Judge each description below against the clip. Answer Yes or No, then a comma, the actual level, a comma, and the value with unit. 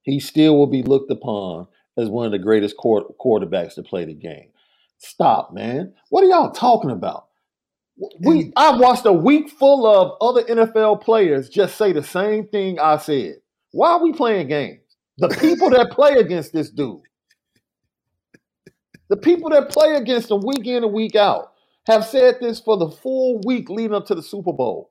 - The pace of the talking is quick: No, average, 180 wpm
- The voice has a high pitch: Yes, high, 220 Hz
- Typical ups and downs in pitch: No, wide, 8.7 semitones